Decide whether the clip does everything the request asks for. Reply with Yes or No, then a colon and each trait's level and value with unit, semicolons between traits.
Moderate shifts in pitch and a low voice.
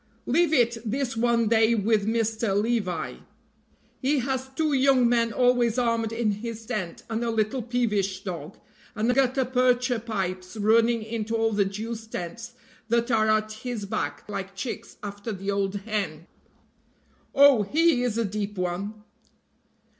No: average, 3.0 semitones; high, 225 Hz